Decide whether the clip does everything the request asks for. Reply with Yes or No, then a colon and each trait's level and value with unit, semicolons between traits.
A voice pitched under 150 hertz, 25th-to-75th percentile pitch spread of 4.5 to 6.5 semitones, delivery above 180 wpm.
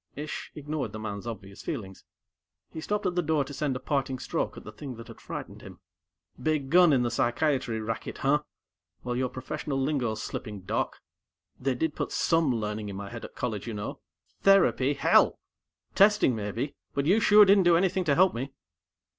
Yes: low, 135 Hz; wide, 5.5 semitones; average, 190 wpm